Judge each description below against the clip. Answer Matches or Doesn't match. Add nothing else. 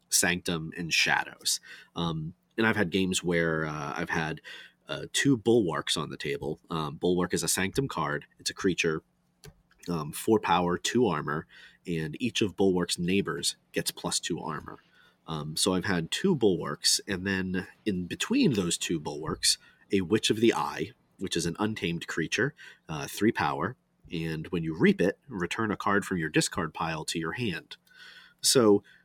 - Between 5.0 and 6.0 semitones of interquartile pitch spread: Doesn't match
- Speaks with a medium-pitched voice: Doesn't match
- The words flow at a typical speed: Matches